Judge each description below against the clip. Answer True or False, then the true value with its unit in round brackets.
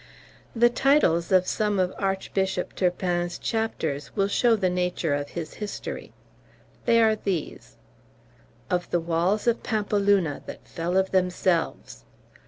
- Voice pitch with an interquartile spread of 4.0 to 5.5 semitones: False (3.3 semitones)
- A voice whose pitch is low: False (185 Hz)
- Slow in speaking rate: True (130 wpm)